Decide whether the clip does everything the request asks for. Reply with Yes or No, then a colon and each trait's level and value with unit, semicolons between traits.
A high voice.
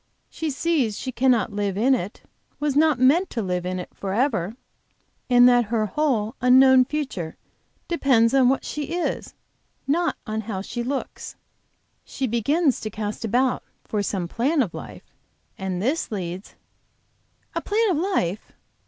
Yes: high, 245 Hz